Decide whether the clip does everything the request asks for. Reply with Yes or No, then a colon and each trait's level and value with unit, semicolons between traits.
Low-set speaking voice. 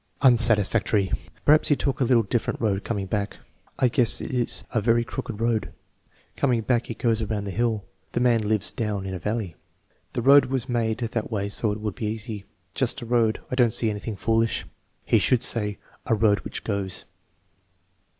Yes: low, 115 Hz